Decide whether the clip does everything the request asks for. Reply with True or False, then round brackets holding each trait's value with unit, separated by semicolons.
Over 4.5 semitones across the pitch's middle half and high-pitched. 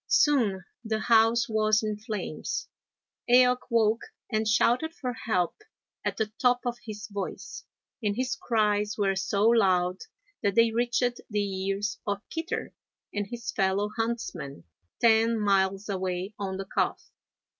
False (2.9 semitones; 215 Hz)